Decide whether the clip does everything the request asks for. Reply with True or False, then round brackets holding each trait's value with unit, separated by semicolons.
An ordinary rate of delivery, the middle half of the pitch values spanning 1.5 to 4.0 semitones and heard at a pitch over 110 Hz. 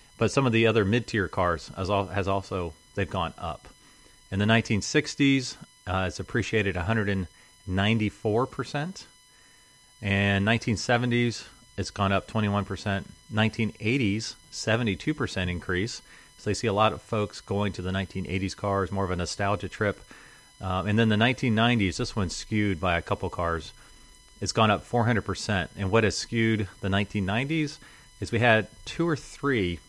False (150 wpm; 3.2 semitones; 105 Hz)